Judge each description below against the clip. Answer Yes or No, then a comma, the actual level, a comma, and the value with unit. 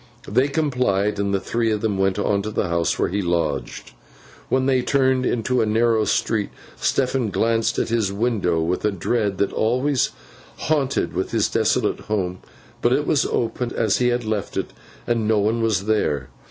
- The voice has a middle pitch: No, low, 110 Hz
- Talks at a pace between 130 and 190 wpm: Yes, average, 175 wpm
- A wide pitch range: No, average, 3.6 semitones